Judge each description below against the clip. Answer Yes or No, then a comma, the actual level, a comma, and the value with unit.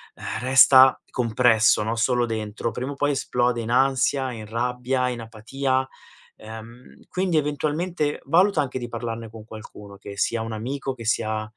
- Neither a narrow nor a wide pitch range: Yes, average, 3.1 semitones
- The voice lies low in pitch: Yes, low, 125 Hz